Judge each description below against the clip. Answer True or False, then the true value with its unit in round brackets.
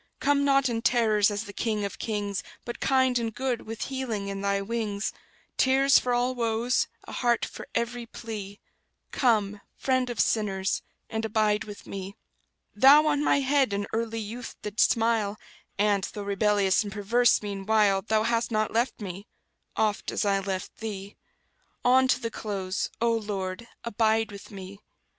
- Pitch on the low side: False (220 Hz)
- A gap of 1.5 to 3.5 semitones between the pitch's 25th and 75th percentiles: True (2.9 semitones)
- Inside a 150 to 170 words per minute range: True (165 wpm)